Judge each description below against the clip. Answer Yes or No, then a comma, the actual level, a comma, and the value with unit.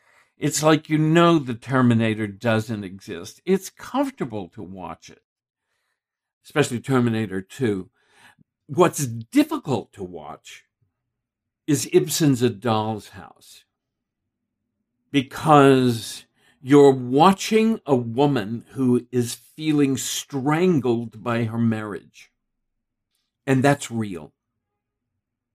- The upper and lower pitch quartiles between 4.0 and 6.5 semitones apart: Yes, average, 4.3 semitones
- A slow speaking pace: Yes, slow, 95 wpm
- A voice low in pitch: Yes, low, 125 Hz